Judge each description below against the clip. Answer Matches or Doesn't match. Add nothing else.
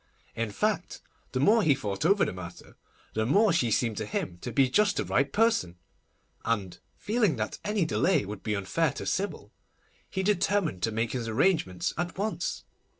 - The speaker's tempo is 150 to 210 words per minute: Matches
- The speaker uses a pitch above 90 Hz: Matches